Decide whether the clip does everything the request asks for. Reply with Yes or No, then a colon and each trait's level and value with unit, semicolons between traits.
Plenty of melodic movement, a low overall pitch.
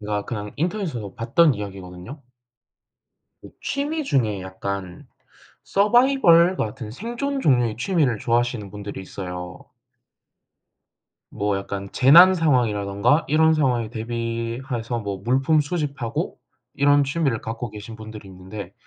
Yes: wide, 6.7 semitones; low, 120 Hz